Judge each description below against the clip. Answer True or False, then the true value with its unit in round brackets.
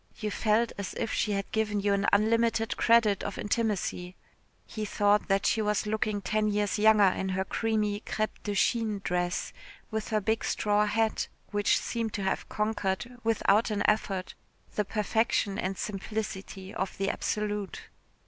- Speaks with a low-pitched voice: False (210 Hz)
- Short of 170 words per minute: True (160 wpm)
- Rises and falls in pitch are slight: True (1.7 semitones)